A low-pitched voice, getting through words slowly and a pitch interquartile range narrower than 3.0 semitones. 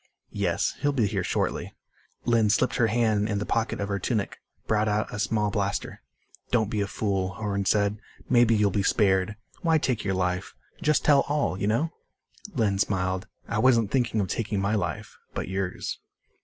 No: low, 105 Hz; average, 185 wpm; narrow, 2.6 semitones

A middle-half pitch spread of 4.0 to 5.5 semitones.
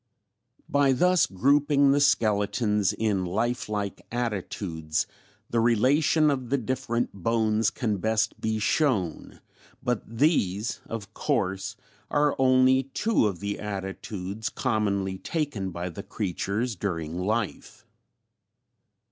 Yes: average, 4.6 semitones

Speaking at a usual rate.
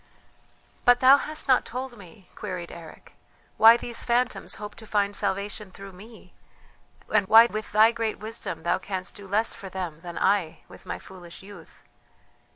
Yes: average, 165 wpm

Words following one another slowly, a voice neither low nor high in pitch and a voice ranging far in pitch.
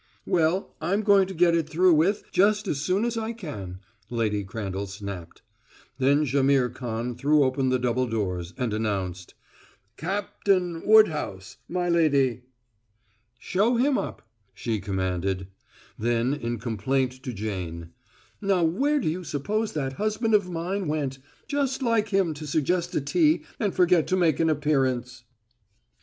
No: average, 150 wpm; medium, 150 Hz; wide, 8.1 semitones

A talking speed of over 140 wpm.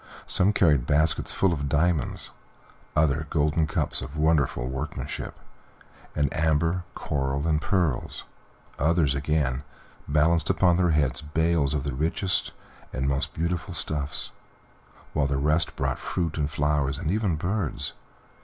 No: slow, 135 wpm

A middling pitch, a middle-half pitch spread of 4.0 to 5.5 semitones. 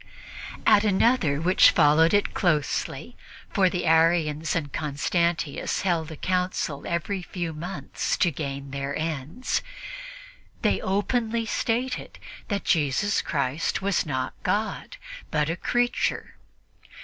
Yes: medium, 170 Hz; average, 4.8 semitones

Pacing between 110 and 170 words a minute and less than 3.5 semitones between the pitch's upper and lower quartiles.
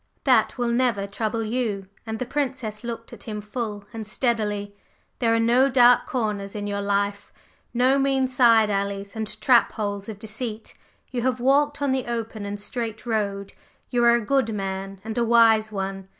No: average, 180 wpm; average, 3.0 semitones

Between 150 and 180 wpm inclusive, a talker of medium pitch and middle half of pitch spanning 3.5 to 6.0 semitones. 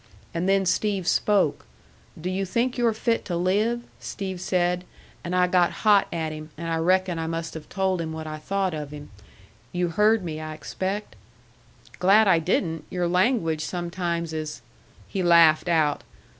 No: average, 175 wpm; medium, 175 Hz; average, 3.0 semitones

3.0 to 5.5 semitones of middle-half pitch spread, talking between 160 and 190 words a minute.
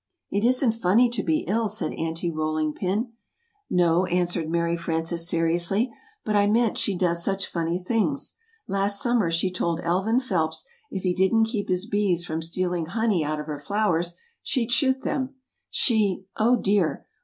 Yes: average, 4.5 semitones; average, 165 wpm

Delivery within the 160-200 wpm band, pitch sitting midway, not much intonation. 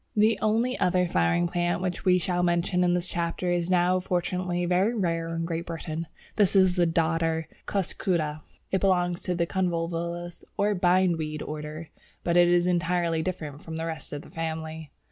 Yes: average, 170 wpm; medium, 175 Hz; narrow, 1.7 semitones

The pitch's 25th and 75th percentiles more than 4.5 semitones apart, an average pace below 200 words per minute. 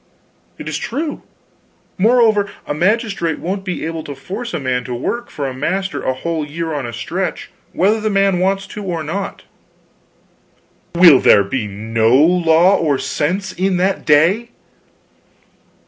Yes: average, 5.3 semitones; average, 150 wpm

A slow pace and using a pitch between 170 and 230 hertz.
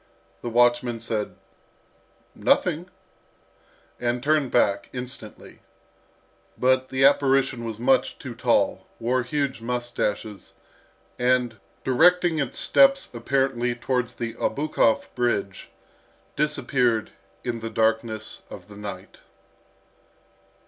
No: slow, 100 wpm; low, 120 Hz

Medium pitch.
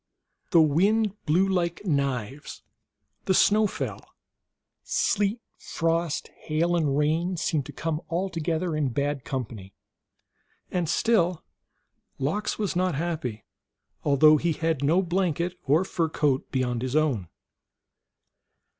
Yes: medium, 160 Hz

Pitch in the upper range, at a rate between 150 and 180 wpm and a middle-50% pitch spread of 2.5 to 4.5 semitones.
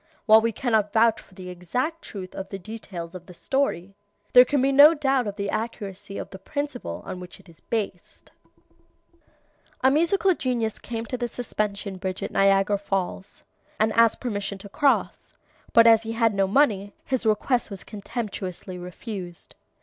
Yes: high, 215 Hz; average, 175 wpm; average, 4.0 semitones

